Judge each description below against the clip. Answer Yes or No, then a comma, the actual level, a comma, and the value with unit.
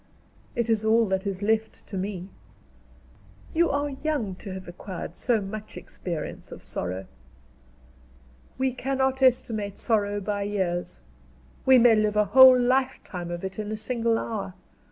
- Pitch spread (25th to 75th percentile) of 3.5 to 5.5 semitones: Yes, average, 4.4 semitones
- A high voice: Yes, high, 215 Hz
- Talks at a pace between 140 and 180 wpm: Yes, average, 150 wpm